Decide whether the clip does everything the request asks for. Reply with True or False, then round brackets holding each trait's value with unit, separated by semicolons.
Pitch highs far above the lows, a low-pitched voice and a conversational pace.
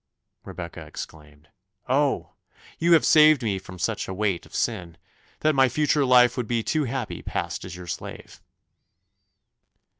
True (7.7 semitones; 120 Hz; 150 wpm)